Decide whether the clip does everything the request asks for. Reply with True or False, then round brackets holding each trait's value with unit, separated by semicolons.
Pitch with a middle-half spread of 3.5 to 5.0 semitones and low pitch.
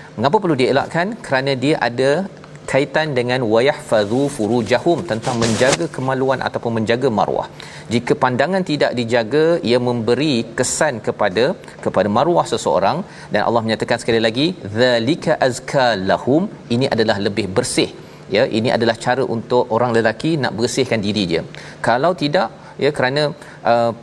True (4.3 semitones; 125 Hz)